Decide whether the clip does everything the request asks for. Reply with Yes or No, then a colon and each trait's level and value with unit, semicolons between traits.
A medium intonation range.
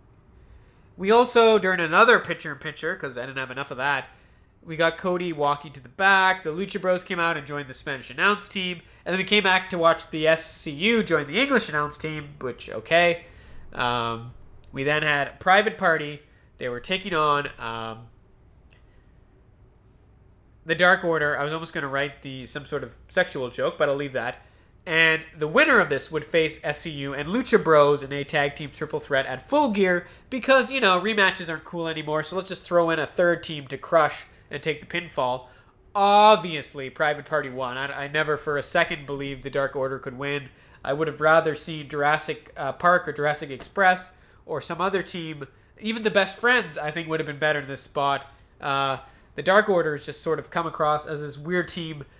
Yes: average, 4.1 semitones